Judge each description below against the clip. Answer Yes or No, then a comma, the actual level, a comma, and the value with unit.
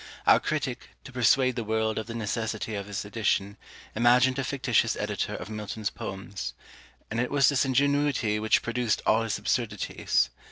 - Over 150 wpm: Yes, average, 165 wpm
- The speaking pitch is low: Yes, low, 115 Hz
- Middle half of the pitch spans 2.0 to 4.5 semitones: Yes, average, 3.2 semitones